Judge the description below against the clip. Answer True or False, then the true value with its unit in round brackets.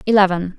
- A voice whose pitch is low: False (190 Hz)